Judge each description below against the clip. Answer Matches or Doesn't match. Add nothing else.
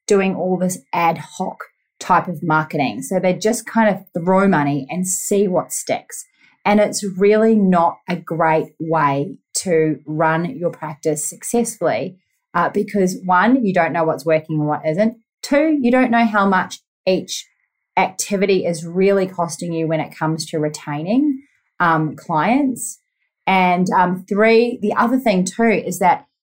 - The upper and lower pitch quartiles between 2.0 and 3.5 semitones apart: Doesn't match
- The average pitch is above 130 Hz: Matches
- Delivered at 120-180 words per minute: Matches